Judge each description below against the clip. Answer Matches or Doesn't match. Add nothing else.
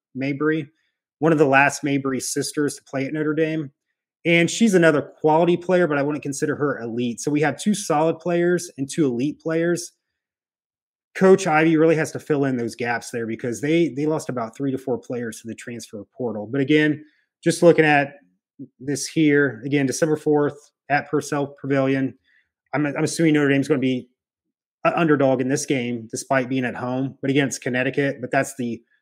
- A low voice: Doesn't match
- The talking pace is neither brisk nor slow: Matches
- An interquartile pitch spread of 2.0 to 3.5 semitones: Matches